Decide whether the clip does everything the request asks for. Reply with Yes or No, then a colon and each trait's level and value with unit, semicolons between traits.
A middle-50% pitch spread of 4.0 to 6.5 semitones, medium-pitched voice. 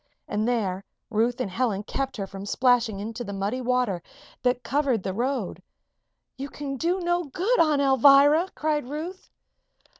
No: average, 5.1 semitones; very high, 255 Hz